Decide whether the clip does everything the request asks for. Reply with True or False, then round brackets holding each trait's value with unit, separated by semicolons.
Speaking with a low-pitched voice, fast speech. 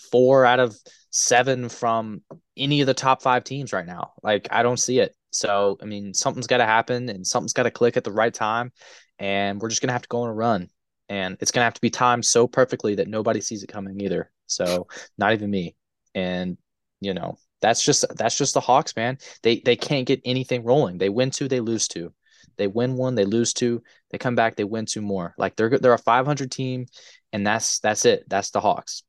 True (120 Hz; 230 wpm)